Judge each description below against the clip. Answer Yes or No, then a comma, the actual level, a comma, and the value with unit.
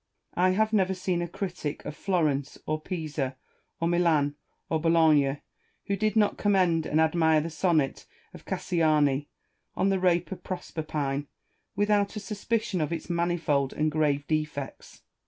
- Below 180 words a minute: Yes, average, 155 wpm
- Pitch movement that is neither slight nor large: Yes, average, 3.6 semitones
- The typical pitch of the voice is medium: Yes, medium, 165 Hz